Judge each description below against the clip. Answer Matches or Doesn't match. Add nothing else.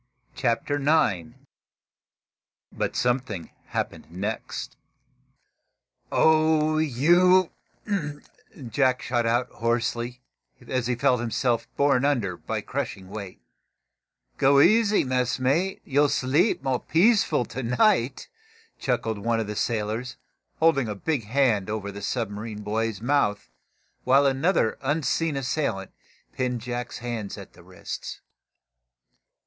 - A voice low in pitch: Matches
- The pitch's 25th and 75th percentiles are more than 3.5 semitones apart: Matches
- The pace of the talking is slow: Matches